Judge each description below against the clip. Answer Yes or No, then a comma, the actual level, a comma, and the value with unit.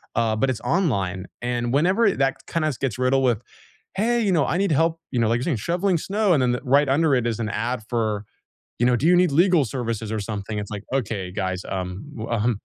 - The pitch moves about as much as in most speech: No, wide, 6.7 semitones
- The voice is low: Yes, low, 125 Hz